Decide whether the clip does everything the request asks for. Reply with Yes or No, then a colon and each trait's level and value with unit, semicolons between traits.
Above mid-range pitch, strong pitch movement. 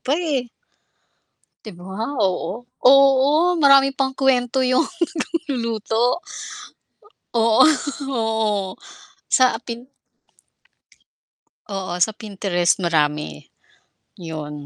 Yes: high, 230 Hz; wide, 5.9 semitones